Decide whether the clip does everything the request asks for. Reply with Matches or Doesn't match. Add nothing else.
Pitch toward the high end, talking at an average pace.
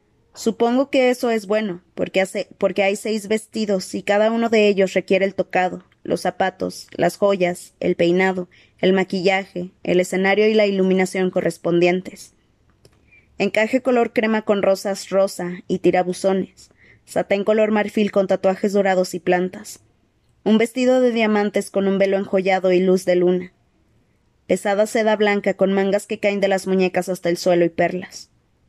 Matches